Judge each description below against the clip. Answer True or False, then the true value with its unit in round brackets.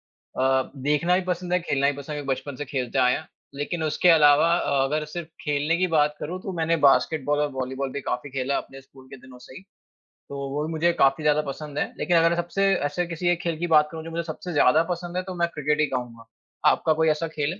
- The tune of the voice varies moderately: True (3.4 semitones)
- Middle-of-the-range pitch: True (150 Hz)